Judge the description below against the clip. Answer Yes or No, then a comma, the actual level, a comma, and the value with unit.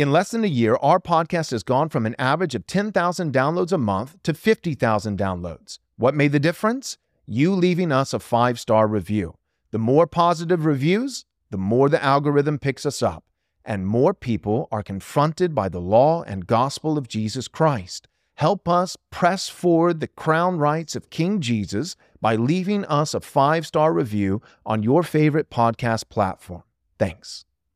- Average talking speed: Yes, average, 170 wpm